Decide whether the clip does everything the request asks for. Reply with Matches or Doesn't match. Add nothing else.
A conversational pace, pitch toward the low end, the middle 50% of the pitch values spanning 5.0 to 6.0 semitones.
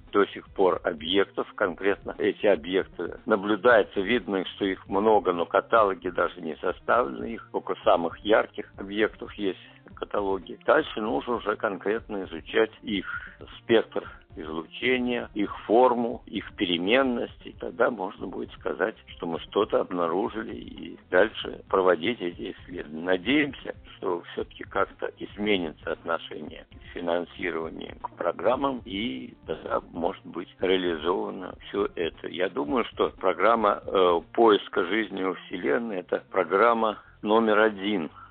Doesn't match